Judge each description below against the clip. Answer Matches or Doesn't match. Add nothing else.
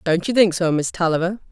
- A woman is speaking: Matches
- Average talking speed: Doesn't match